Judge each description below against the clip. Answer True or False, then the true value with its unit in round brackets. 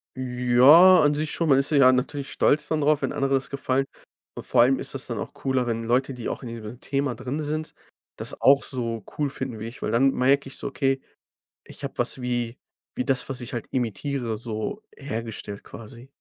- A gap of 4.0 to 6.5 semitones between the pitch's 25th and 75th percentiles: False (2.7 semitones)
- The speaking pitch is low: True (130 Hz)